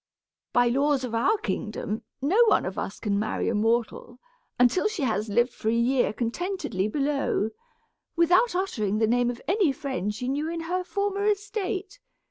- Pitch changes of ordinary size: No, wide, 8.3 semitones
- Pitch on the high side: Yes, very high, 265 Hz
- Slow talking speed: No, average, 175 wpm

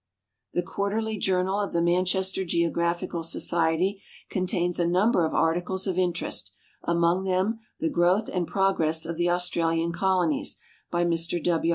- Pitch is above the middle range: No, medium, 175 Hz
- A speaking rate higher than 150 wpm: No, average, 145 wpm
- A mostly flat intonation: Yes, narrow, 2.0 semitones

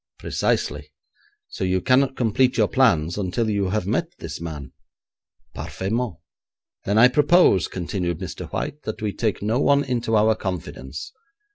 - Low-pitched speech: Yes, low, 105 Hz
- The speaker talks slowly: No, average, 145 wpm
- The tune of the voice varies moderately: No, wide, 5.9 semitones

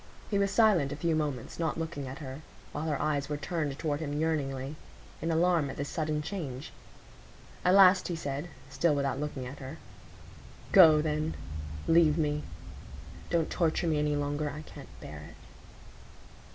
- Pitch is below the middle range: No, medium, 150 Hz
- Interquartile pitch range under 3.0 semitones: Yes, narrow, 2.6 semitones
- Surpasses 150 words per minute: Yes, average, 160 wpm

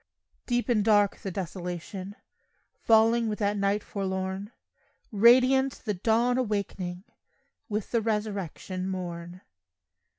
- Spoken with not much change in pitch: No, average, 3.0 semitones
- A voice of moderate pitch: No, high, 205 Hz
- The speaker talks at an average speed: No, slow, 105 wpm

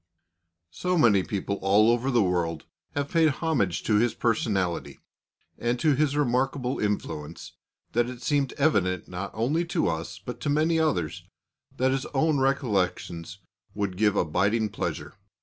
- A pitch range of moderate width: No, wide, 6.8 semitones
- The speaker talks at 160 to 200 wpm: No, average, 150 wpm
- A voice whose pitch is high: No, low, 115 Hz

